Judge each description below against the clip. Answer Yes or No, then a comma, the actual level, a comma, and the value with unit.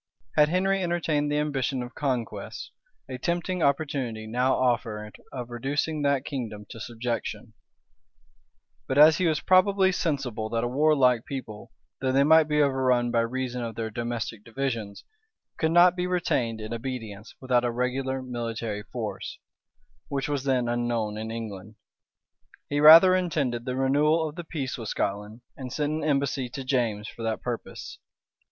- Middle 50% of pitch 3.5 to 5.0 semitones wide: Yes, average, 4.2 semitones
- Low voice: Yes, low, 130 Hz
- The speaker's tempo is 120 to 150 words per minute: No, average, 160 wpm